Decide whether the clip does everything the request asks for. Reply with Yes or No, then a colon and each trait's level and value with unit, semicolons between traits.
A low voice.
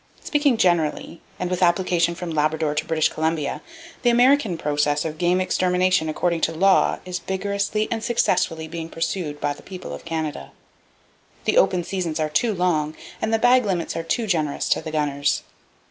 No: medium, 175 Hz